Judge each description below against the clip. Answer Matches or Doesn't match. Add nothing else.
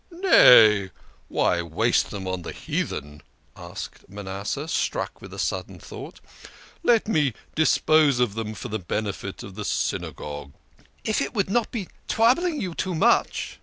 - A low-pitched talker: Matches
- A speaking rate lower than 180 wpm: Matches